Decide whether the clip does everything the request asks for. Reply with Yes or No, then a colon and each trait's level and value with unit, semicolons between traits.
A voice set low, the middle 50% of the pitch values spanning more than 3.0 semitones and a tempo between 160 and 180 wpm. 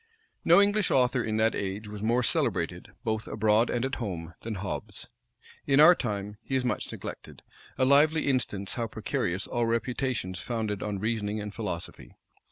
Yes: low, 110 Hz; average, 3.7 semitones; average, 170 wpm